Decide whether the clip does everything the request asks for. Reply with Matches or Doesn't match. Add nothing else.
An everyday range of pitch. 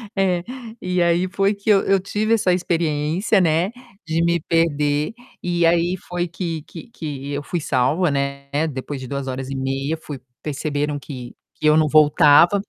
Matches